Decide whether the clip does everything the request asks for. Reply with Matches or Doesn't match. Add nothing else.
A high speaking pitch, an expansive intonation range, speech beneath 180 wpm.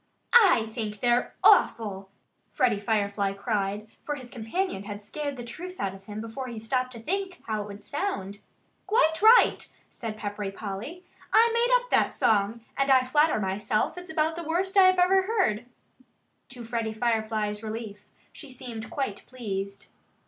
Matches